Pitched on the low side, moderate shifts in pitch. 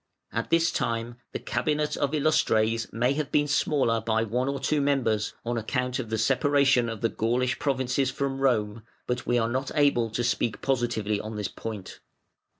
Yes: low, 125 Hz; average, 3.5 semitones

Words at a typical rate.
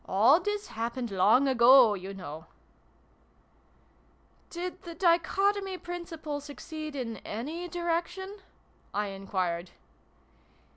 No: slow, 110 wpm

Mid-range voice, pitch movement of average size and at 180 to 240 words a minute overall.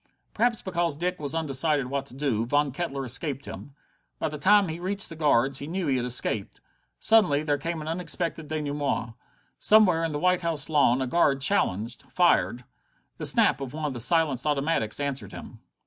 Yes: medium, 150 Hz; average, 3.8 semitones; average, 190 wpm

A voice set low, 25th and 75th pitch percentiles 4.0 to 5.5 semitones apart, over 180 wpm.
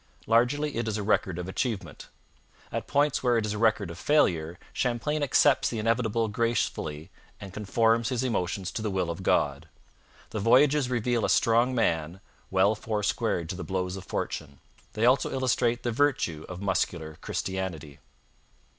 No: low, 110 Hz; average, 4.8 semitones; average, 165 wpm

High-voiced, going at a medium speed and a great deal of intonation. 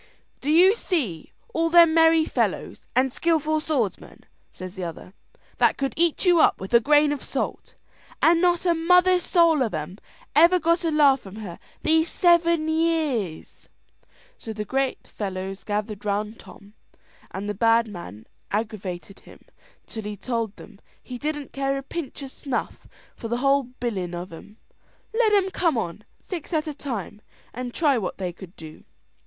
Yes: very high, 265 Hz; average, 170 wpm; wide, 7.9 semitones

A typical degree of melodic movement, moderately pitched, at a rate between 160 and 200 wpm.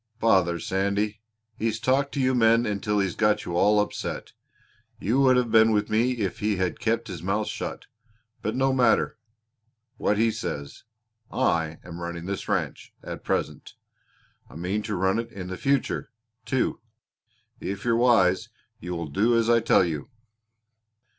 No: average, 3.8 semitones; low, 105 Hz; average, 165 wpm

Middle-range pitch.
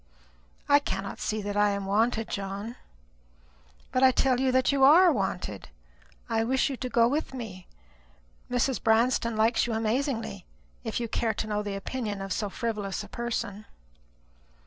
No: high, 225 Hz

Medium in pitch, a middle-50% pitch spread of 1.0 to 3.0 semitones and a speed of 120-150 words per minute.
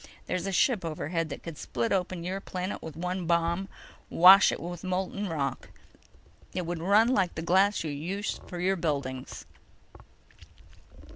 Yes: medium, 175 Hz; average, 2.7 semitones; average, 145 wpm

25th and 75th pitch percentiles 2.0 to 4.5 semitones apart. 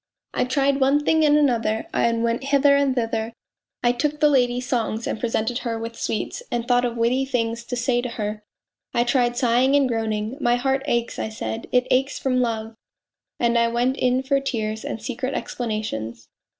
Yes: narrow, 2.6 semitones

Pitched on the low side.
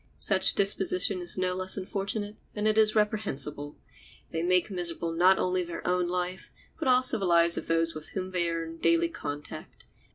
No: medium, 180 Hz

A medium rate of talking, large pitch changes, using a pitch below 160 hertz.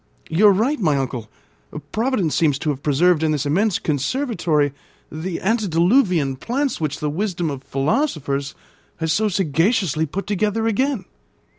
No: average, 145 wpm; wide, 6.5 semitones; medium, 170 Hz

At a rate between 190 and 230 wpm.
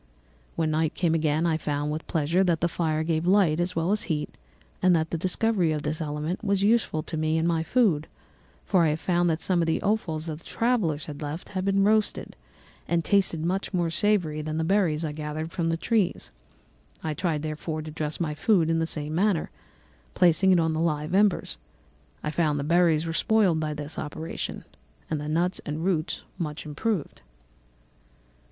Yes: average, 195 wpm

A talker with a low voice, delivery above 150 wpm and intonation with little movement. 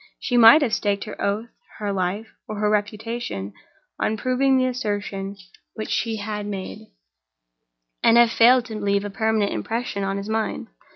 No: high, 215 Hz; average, 165 wpm; narrow, 2.3 semitones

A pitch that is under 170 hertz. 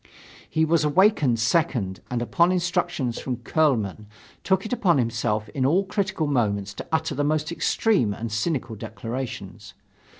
Yes: medium, 140 Hz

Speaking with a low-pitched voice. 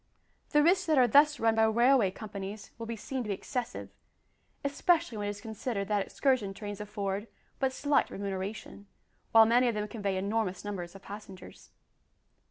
No: high, 215 Hz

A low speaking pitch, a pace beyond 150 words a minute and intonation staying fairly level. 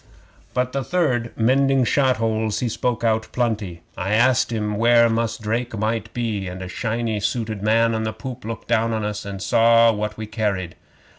Yes: low, 115 Hz; average, 190 wpm; narrow, 1.8 semitones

